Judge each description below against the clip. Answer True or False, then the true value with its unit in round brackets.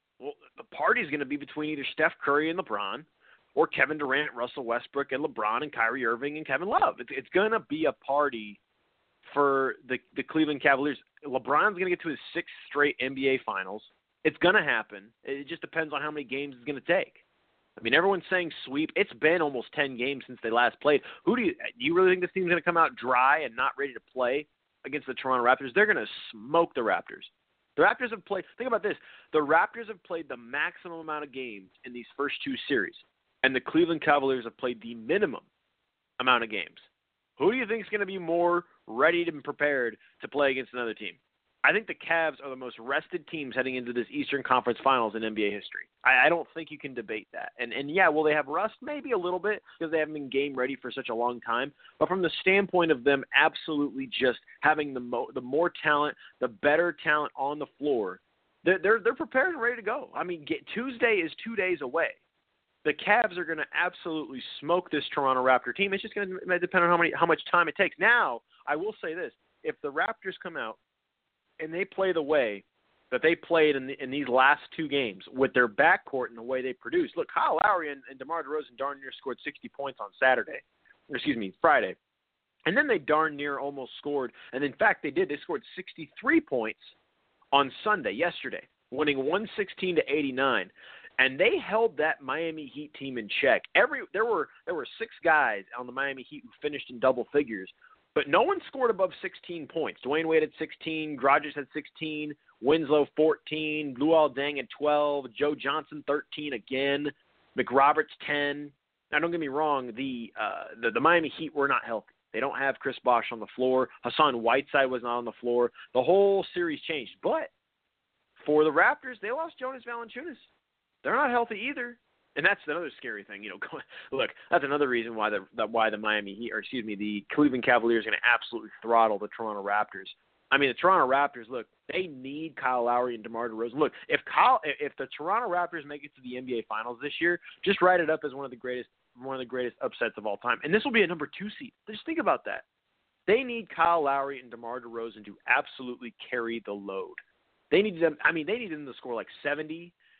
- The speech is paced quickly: True (220 wpm)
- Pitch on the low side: False (150 Hz)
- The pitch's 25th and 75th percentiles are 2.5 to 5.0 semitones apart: False (5.5 semitones)